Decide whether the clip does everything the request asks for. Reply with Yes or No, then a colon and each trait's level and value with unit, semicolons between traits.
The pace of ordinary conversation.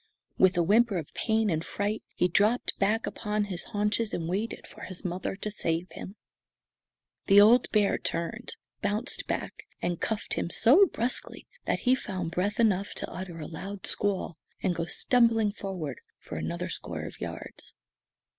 Yes: average, 165 wpm